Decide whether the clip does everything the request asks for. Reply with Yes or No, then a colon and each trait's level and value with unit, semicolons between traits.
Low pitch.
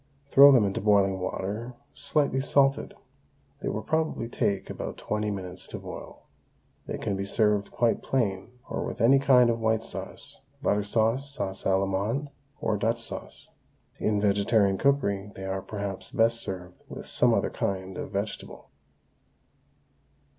Yes: low, 105 Hz